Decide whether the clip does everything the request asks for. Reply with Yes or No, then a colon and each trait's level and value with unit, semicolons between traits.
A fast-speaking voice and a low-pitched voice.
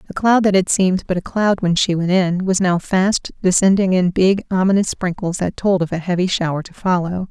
No: fast, 230 wpm; medium, 185 Hz